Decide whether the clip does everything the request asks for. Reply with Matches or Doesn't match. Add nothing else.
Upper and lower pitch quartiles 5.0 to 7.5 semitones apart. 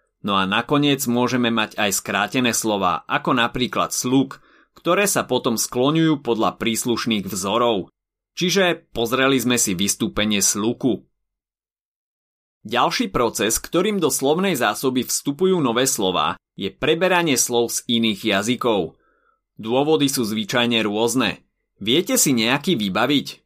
Matches